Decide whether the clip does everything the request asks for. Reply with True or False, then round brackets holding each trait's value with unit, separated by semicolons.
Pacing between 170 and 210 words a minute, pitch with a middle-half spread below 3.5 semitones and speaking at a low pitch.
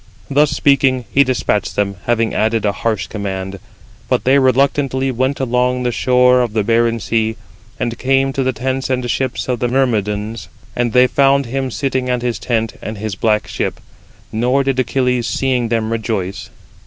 True (180 wpm; 2.9 semitones; 125 Hz)